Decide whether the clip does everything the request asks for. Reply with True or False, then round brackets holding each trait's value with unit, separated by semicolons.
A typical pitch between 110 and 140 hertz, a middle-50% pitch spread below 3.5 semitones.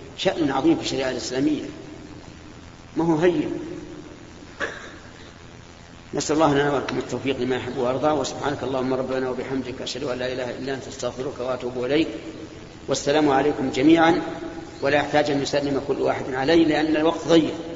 False (135 Hz; 4.2 semitones)